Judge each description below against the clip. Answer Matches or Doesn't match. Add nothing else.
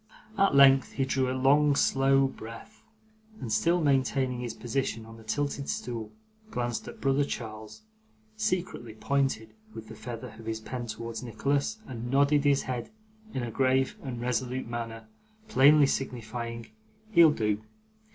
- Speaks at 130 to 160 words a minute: Matches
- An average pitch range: Matches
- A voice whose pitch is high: Doesn't match